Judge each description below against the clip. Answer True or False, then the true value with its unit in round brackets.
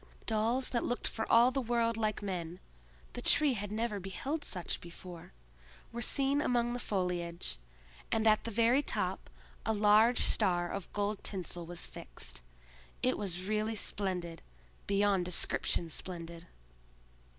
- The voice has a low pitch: False (200 Hz)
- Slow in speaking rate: True (130 wpm)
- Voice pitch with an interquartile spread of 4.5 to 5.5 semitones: True (5.1 semitones)